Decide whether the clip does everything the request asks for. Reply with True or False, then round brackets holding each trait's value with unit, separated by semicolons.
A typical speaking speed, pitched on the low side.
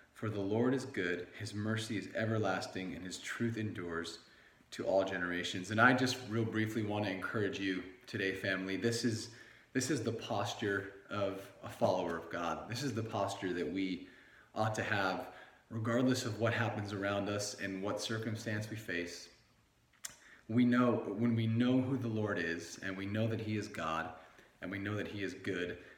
True (185 wpm; 105 Hz)